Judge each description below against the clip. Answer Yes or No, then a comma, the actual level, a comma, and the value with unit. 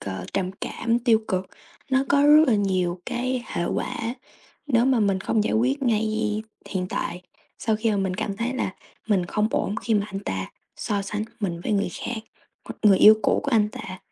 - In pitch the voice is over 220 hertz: No, high, 210 Hz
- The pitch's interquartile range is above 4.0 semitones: No, average, 3.6 semitones